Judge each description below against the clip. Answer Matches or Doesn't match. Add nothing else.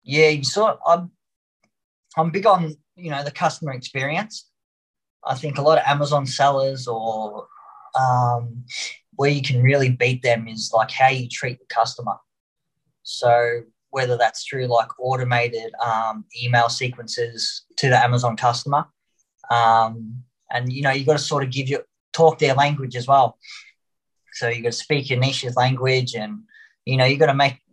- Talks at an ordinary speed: Doesn't match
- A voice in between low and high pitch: Doesn't match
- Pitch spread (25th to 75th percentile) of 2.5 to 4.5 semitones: Matches